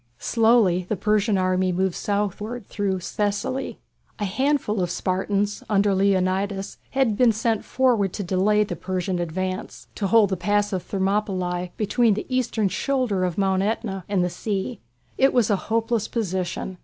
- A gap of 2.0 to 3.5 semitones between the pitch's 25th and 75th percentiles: Yes, narrow, 2.6 semitones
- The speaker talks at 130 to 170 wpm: Yes, average, 155 wpm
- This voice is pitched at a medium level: No, high, 200 Hz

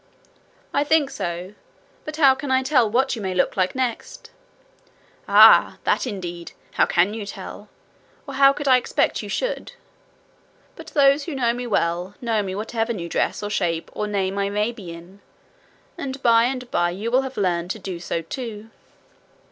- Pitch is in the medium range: No, high, 220 Hz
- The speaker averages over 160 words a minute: Yes, average, 180 wpm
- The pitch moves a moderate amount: No, wide, 5.8 semitones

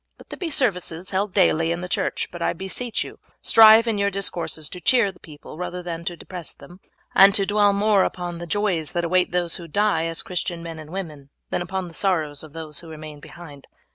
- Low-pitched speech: No, medium, 175 Hz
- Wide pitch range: No, average, 3.2 semitones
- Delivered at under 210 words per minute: No, fast, 225 wpm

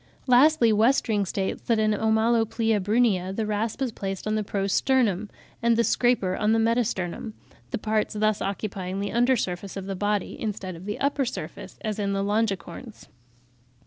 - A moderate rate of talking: Yes, average, 175 wpm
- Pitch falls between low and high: No, high, 215 Hz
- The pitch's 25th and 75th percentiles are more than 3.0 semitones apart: No, average, 2.7 semitones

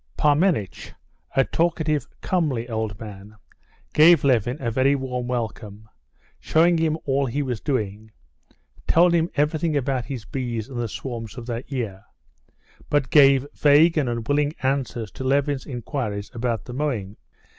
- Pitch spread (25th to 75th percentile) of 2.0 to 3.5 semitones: No, average, 4.2 semitones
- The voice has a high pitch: No, low, 130 Hz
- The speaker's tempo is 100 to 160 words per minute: Yes, average, 145 wpm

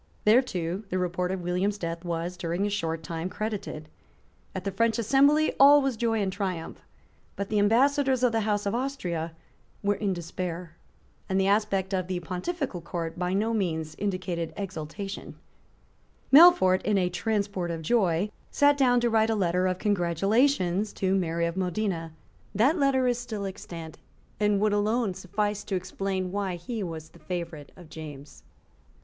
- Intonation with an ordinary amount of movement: Yes, average, 3.9 semitones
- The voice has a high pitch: Yes, high, 195 Hz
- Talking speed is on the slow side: No, average, 165 wpm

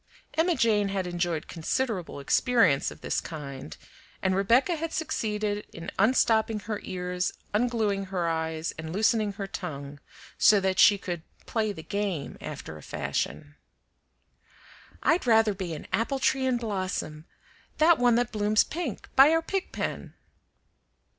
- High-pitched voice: Yes, high, 205 Hz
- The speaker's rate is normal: Yes, average, 145 wpm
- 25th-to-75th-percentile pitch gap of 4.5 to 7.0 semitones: Yes, average, 5.2 semitones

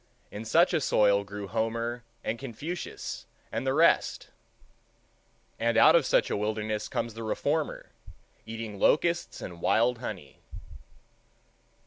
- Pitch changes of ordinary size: Yes, average, 4.0 semitones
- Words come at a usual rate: No, slow, 125 wpm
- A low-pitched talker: Yes, low, 115 Hz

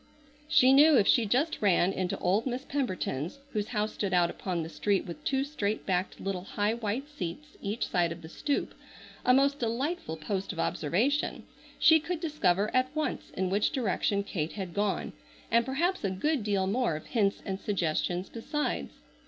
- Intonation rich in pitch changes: Yes, wide, 6.2 semitones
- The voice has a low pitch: No, high, 210 Hz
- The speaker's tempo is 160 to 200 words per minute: Yes, average, 180 wpm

